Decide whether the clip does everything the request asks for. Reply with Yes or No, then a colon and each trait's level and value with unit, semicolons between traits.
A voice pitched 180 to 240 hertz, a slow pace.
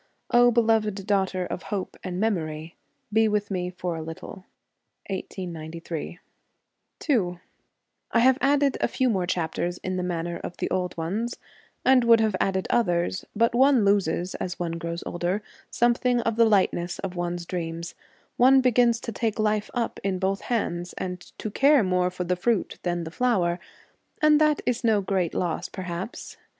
No: high, 190 Hz; average, 165 wpm